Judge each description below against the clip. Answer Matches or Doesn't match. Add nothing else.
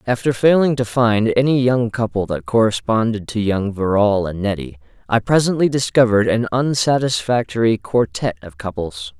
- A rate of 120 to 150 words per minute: Matches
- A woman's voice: Doesn't match